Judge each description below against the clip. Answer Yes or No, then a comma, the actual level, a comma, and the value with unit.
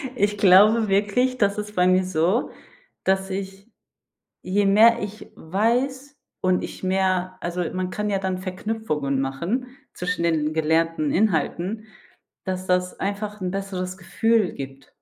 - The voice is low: No, high, 190 Hz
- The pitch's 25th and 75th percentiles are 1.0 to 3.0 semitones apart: Yes, narrow, 2.6 semitones